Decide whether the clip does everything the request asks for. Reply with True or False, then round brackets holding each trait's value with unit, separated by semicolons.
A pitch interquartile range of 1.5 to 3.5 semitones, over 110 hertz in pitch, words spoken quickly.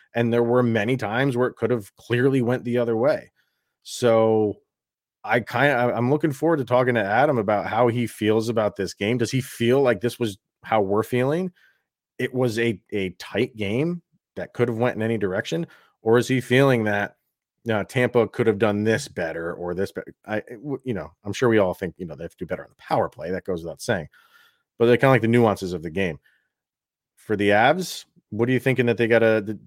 True (2.8 semitones; 120 Hz; 235 wpm)